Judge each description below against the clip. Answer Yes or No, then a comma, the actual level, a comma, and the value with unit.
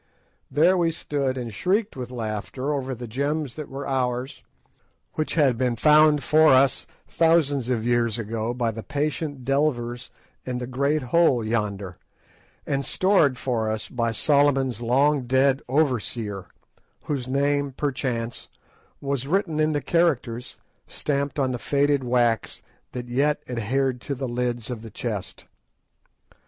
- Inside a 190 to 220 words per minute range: No, average, 145 wpm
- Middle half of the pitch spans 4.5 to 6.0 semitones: No, average, 3.3 semitones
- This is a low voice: Yes, low, 130 Hz